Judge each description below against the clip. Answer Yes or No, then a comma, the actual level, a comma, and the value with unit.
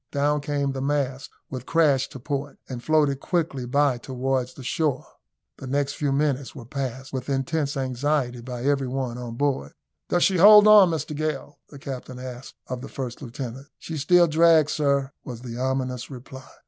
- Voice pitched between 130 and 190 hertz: Yes, low, 135 Hz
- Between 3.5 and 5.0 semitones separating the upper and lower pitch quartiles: No, narrow, 2.4 semitones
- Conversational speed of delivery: Yes, average, 180 wpm